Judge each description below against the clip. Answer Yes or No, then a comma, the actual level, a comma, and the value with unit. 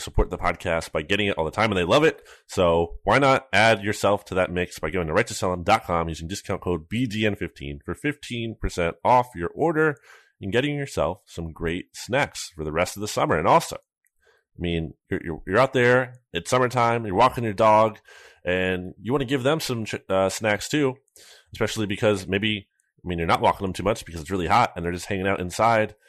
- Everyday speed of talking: No, fast, 215 wpm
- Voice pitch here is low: Yes, low, 100 Hz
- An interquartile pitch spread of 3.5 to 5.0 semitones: Yes, average, 4.7 semitones